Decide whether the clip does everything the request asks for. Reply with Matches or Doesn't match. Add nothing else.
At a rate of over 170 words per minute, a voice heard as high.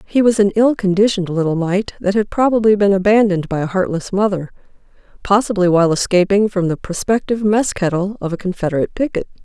Matches